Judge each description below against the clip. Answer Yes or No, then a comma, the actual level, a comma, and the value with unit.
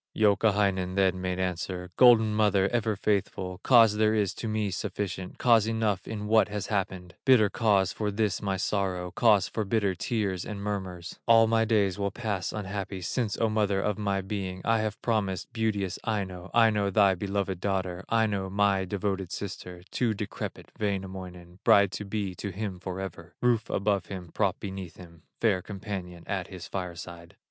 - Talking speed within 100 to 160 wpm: No, average, 170 wpm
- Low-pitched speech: Yes, low, 100 Hz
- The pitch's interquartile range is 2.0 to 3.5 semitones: Yes, narrow, 2.5 semitones